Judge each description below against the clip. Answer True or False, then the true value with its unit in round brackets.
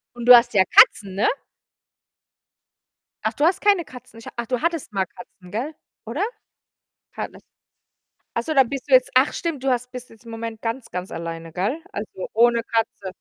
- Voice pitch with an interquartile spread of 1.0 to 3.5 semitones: False (4.1 semitones)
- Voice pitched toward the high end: True (235 Hz)